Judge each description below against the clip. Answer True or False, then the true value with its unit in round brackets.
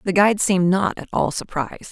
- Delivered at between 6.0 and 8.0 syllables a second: True (6.1 syllables/s)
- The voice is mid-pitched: True (180 Hz)